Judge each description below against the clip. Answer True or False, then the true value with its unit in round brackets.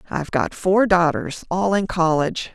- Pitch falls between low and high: True (175 Hz)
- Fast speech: False (140 wpm)